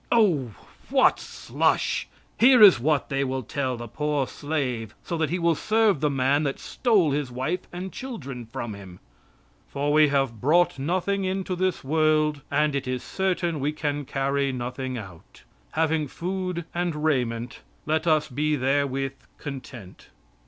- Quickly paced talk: No, average, 150 wpm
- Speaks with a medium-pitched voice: Yes, medium, 145 Hz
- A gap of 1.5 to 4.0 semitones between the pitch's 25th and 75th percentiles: No, average, 4.4 semitones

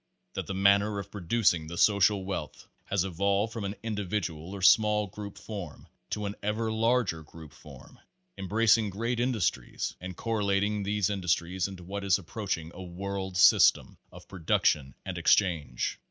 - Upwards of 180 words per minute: No, average, 155 wpm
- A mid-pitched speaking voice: No, low, 100 Hz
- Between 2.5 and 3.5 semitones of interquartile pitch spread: Yes, average, 2.8 semitones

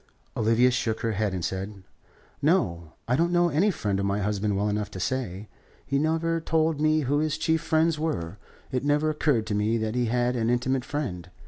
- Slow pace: No, fast, 205 wpm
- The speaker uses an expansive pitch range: Yes, wide, 6.8 semitones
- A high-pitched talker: No, low, 125 Hz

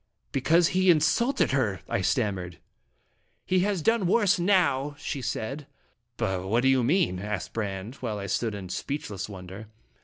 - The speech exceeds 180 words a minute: No, average, 160 wpm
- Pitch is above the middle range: No, low, 125 Hz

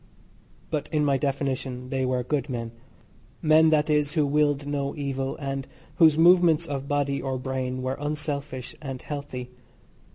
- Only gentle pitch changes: Yes, narrow, 2.3 semitones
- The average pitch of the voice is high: No, medium, 140 Hz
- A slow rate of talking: No, average, 155 wpm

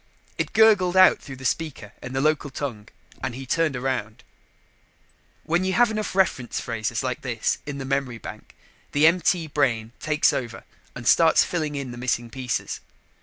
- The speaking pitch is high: No, low, 135 Hz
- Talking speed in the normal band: Yes, average, 170 wpm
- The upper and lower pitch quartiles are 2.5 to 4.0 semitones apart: No, average, 5.0 semitones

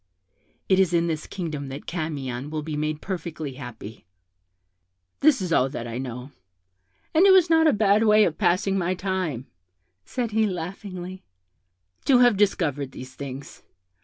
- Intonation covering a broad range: Yes, wide, 6.1 semitones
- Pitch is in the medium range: Yes, medium, 170 Hz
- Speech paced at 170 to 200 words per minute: No, average, 160 wpm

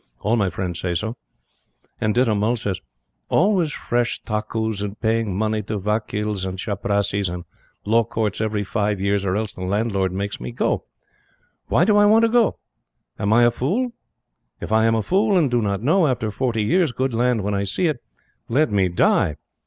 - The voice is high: No, low, 110 Hz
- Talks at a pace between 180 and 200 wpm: Yes, average, 190 wpm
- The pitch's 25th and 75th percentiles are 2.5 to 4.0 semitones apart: Yes, average, 3.4 semitones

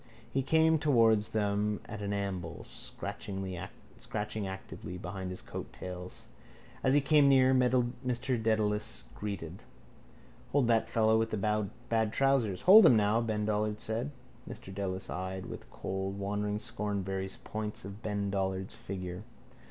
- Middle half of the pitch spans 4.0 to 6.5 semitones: No, average, 3.0 semitones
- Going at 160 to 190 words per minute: No, slow, 135 wpm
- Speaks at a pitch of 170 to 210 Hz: No, low, 105 Hz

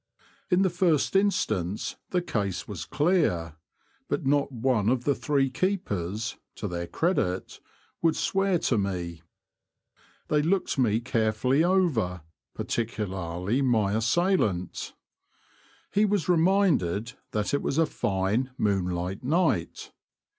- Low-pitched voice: Yes, low, 120 Hz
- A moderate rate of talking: No, slow, 120 wpm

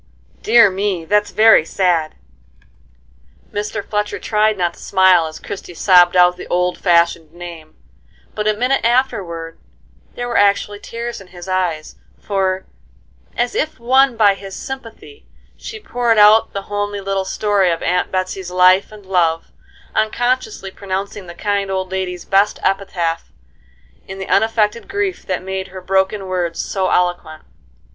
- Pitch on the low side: No, high, 195 Hz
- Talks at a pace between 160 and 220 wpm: No, average, 150 wpm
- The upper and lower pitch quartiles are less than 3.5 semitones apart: Yes, average, 2.9 semitones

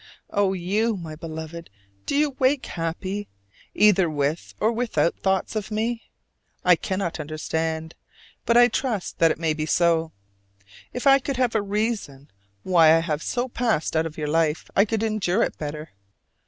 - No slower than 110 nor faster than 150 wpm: No, average, 170 wpm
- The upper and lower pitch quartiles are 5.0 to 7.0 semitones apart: Yes, wide, 5.6 semitones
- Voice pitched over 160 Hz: Yes, medium, 185 Hz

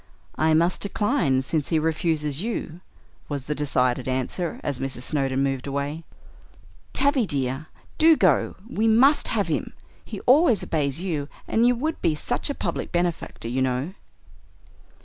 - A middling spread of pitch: No, wide, 7.4 semitones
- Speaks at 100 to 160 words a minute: Yes, average, 150 wpm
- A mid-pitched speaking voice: Yes, medium, 155 Hz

